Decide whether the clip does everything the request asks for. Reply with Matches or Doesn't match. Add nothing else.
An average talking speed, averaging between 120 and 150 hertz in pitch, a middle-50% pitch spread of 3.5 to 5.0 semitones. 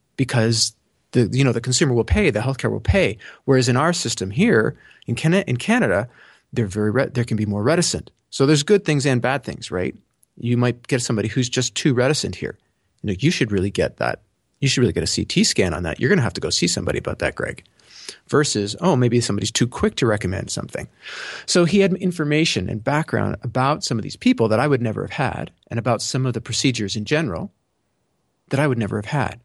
Doesn't match